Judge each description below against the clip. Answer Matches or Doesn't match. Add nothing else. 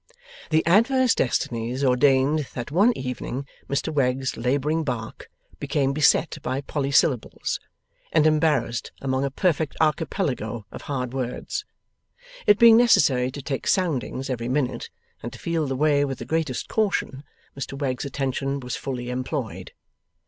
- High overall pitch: Doesn't match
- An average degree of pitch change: Matches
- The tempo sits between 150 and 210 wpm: Doesn't match